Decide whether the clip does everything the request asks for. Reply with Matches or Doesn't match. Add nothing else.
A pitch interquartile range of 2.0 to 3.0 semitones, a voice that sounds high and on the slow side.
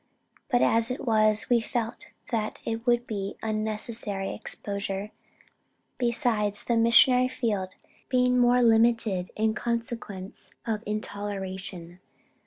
Matches